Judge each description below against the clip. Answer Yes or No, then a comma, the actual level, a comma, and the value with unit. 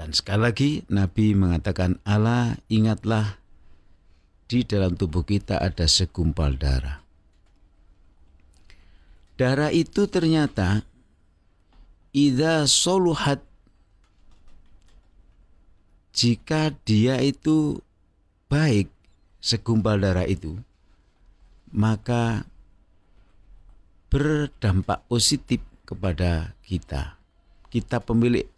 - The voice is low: Yes, very low, 95 Hz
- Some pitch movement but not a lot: No, wide, 6.6 semitones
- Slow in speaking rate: Yes, slow, 70 wpm